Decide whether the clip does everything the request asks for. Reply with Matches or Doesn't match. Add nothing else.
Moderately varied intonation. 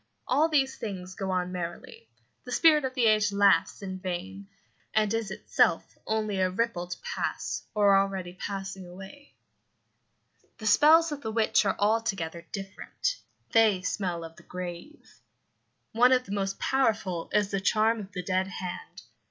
Matches